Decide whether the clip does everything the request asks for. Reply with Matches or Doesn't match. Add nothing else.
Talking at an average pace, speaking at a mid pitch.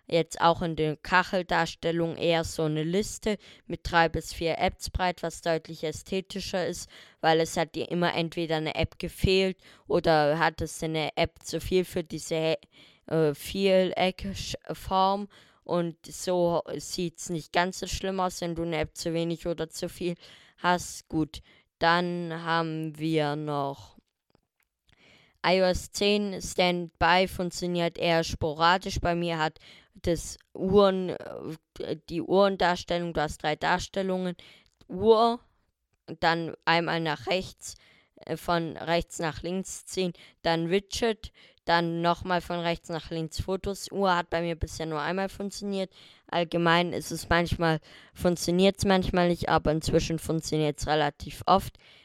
Matches